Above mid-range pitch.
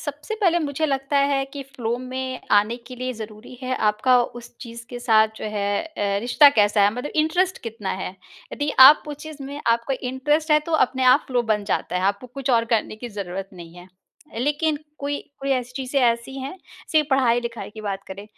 Yes: very high, 250 Hz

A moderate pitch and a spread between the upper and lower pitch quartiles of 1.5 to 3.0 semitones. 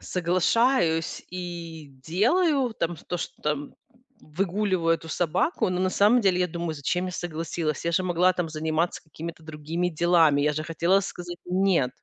Yes: medium, 175 Hz; narrow, 2.4 semitones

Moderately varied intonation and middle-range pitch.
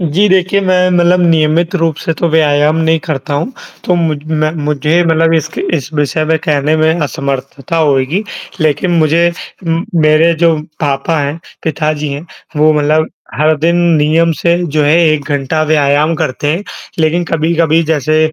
No: narrow, 2.0 semitones; medium, 155 Hz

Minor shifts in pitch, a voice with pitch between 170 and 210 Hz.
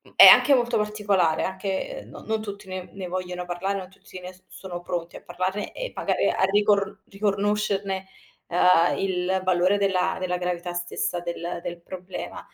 Yes: narrow, 2.0 semitones; high, 190 Hz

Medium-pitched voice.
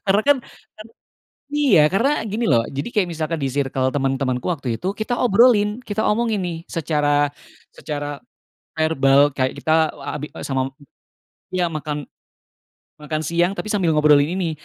Yes: medium, 160 Hz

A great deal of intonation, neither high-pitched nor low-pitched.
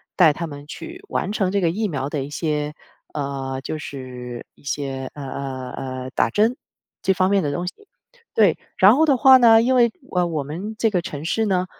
Yes: wide, 6.8 semitones; medium, 165 Hz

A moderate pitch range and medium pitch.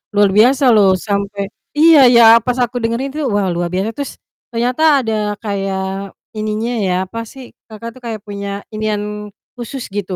No: average, 3.5 semitones; high, 215 Hz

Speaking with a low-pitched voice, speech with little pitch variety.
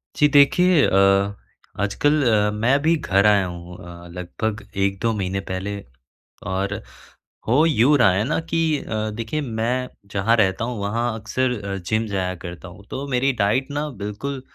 No: low, 110 Hz; average, 5.3 semitones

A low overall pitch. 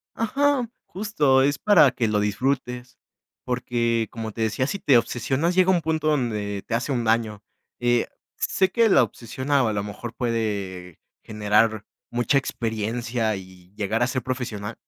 Yes: low, 120 Hz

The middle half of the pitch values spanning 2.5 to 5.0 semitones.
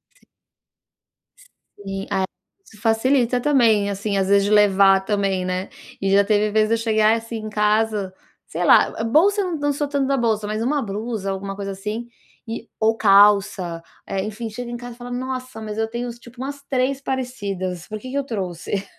Yes: average, 3.5 semitones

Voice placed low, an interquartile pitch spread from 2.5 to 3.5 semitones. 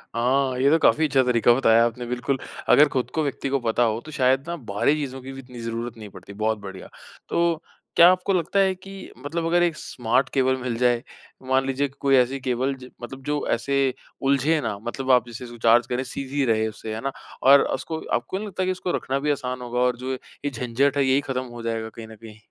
Yes: low, 130 Hz; average, 3.0 semitones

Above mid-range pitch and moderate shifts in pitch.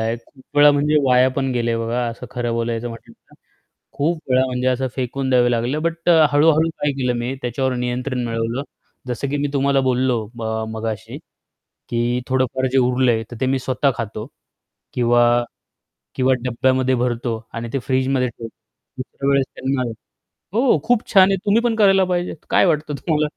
No: low, 130 Hz; average, 3.0 semitones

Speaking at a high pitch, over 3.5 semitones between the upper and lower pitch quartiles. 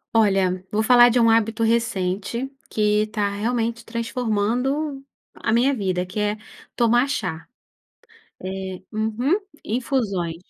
No: high, 225 Hz; average, 3.0 semitones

